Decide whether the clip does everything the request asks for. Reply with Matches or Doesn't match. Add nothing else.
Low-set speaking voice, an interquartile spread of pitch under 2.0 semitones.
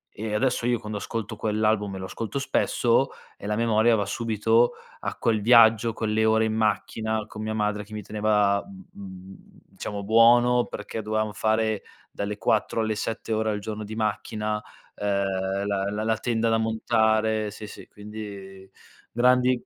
Matches